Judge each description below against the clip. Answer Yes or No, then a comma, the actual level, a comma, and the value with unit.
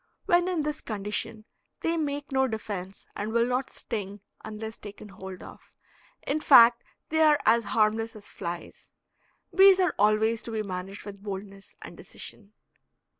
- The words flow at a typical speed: Yes, average, 155 wpm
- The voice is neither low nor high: No, high, 220 Hz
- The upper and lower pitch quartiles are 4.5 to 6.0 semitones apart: Yes, average, 5.0 semitones